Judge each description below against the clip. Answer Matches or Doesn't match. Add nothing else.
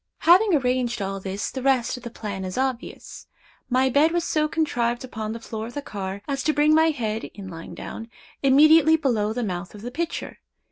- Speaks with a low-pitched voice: Doesn't match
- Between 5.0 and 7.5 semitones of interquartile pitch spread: Matches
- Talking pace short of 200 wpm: Doesn't match